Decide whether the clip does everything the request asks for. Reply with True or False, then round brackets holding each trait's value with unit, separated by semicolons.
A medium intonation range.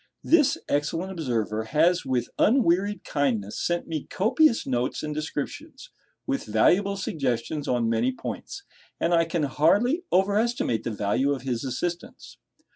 False (7.9 semitones)